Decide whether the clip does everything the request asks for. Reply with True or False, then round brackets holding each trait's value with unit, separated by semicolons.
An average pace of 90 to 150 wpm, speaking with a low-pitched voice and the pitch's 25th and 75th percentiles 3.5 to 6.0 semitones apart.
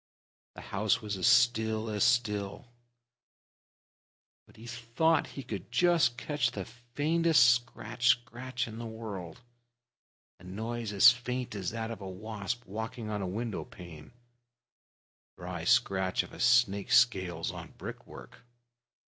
False (140 wpm; 115 Hz; 3.1 semitones)